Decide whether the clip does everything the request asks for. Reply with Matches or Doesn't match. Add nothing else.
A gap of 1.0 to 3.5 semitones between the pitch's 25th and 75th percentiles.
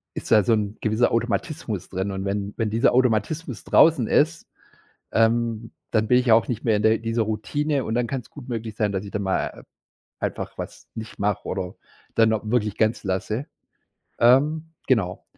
Matches